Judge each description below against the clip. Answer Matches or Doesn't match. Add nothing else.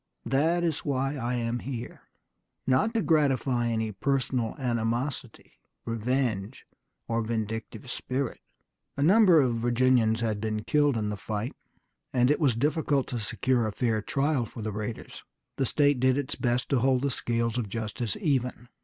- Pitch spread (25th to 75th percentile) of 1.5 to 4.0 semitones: Matches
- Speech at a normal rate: Matches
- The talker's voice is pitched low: Matches